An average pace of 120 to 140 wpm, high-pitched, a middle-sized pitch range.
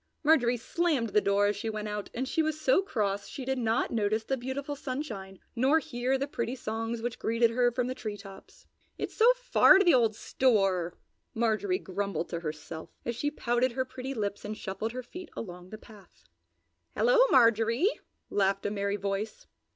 No: average, 190 wpm; high, 230 Hz; average, 4.4 semitones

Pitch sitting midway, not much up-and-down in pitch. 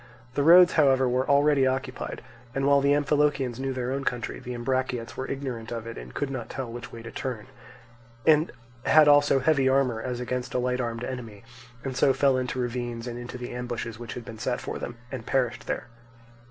No: low, 130 Hz; narrow, 2.2 semitones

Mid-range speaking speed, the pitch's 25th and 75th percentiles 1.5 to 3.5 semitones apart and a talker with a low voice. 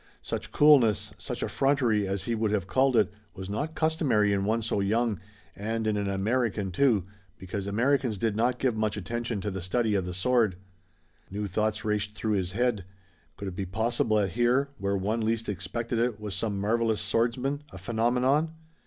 Yes: average, 185 wpm; average, 3.2 semitones; low, 110 Hz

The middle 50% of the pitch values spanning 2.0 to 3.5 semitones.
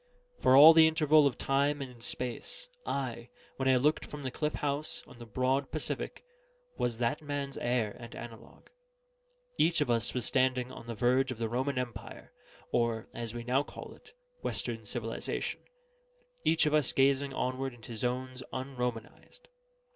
Yes: average, 2.9 semitones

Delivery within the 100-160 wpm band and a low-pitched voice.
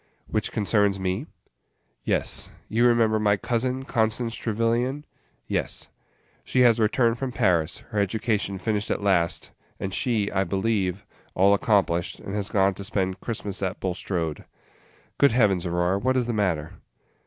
Yes: average, 150 wpm; low, 105 Hz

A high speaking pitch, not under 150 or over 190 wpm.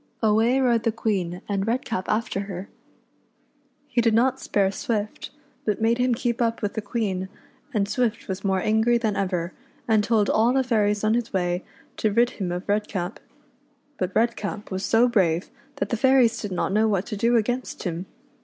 Yes: high, 215 Hz; average, 185 wpm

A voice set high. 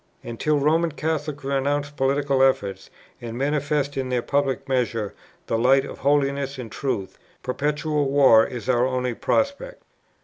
No: low, 135 Hz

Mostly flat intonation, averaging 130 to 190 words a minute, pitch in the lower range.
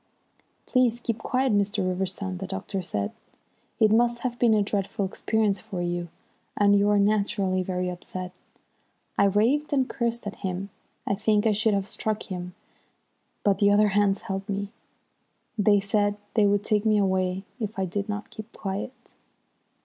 No: narrow, 2.2 semitones; average, 165 wpm; high, 205 Hz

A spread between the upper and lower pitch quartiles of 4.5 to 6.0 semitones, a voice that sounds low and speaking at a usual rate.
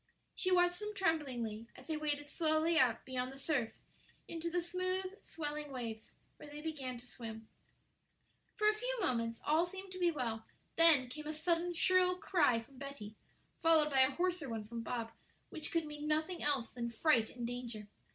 No: wide, 5.6 semitones; very high, 295 Hz; average, 180 wpm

